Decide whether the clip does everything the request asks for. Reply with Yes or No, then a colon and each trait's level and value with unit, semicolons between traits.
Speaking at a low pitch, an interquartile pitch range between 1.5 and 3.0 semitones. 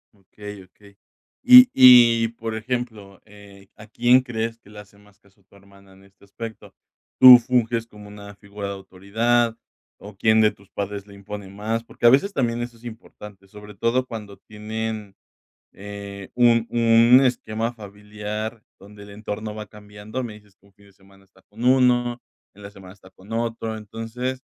Yes: low, 105 Hz; narrow, 2.5 semitones